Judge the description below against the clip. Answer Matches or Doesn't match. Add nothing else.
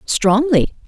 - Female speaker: Matches